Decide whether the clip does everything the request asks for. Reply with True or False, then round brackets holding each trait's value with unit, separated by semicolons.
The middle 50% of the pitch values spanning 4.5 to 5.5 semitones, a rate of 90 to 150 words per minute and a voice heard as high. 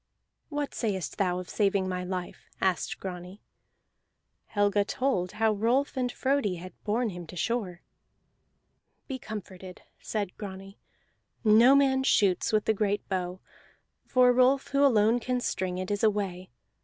True (4.8 semitones; 145 wpm; 205 Hz)